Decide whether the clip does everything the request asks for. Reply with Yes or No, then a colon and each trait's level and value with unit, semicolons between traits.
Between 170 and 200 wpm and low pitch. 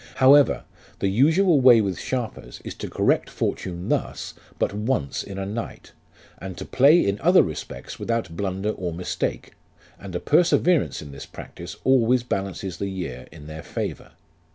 No: average, 160 wpm; low, 100 Hz